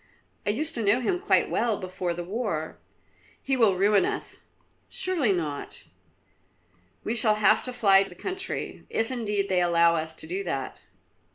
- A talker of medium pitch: No, high, 205 Hz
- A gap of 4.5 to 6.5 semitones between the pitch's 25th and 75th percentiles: Yes, average, 5.1 semitones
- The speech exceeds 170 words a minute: No, average, 165 wpm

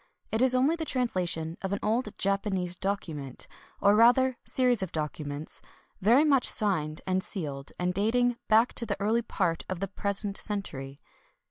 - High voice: Yes, high, 200 Hz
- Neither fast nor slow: Yes, average, 175 wpm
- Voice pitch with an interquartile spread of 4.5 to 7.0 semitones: Yes, average, 5.2 semitones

